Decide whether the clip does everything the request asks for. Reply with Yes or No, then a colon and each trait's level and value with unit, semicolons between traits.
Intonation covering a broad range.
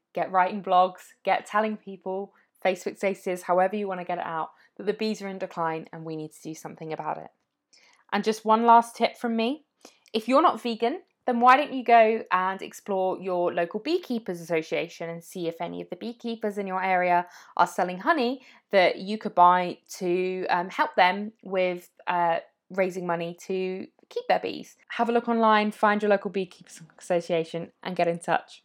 No: average, 3.8 semitones